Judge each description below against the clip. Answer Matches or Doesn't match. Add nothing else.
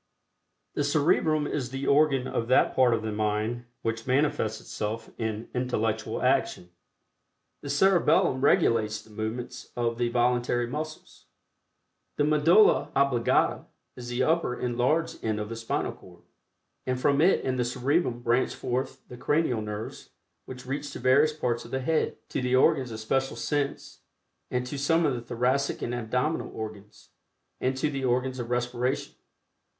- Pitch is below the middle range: Matches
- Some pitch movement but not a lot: Matches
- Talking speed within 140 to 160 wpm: Matches